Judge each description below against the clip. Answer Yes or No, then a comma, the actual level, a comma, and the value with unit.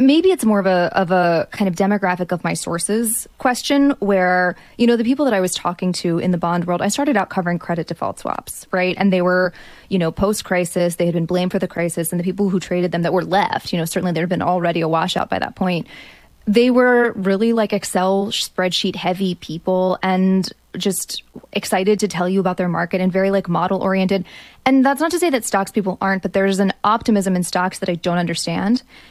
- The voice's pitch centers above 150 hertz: Yes, high, 190 Hz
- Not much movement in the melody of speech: Yes, narrow, 2.3 semitones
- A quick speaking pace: Yes, fast, 230 wpm